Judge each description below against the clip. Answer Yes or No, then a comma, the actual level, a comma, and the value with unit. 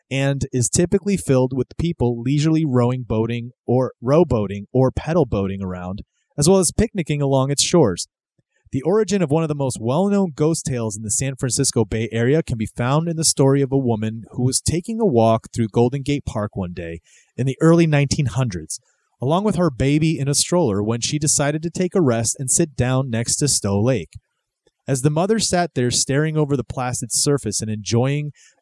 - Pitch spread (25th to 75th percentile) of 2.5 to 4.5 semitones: No, average, 4.9 semitones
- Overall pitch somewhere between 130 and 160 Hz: Yes, low, 135 Hz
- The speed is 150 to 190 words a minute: No, average, 200 wpm